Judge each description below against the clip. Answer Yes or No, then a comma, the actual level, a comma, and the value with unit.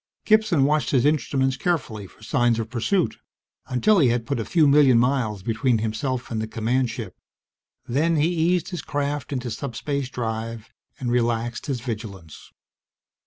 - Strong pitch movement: No, average, 4.2 semitones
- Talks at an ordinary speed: Yes, average, 160 wpm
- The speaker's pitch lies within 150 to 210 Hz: No, low, 125 Hz